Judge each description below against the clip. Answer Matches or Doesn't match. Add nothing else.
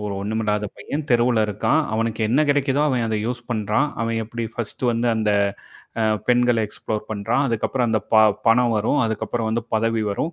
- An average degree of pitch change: Doesn't match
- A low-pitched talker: Matches